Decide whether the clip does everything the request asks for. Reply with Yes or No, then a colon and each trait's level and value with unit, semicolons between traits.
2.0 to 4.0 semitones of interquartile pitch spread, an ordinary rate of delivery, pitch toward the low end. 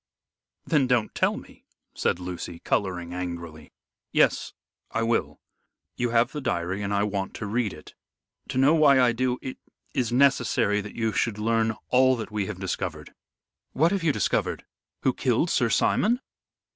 No: average, 4.8 semitones; average, 165 wpm; low, 115 Hz